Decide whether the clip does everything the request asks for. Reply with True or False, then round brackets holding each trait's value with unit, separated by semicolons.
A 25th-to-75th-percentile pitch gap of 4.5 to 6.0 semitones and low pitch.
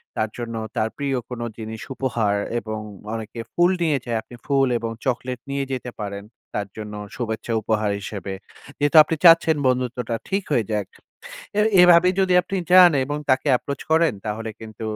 True (4.9 semitones; 125 Hz)